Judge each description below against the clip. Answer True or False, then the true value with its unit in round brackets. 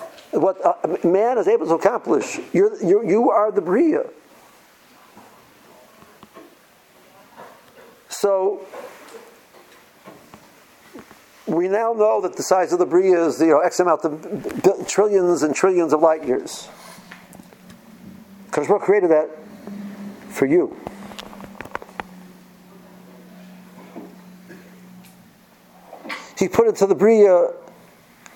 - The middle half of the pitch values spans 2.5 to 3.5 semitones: True (2.8 semitones)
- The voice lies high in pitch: True (195 Hz)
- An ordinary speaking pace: False (100 wpm)